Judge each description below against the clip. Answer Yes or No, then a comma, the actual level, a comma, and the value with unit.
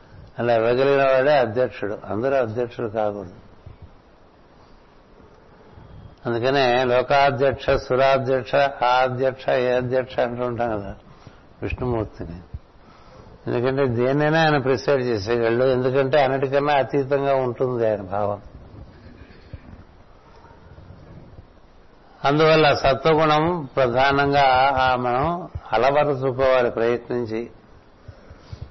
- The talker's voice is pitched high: No, low, 130 Hz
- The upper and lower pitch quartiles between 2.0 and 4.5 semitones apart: Yes, average, 2.9 semitones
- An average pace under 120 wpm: Yes, average, 75 wpm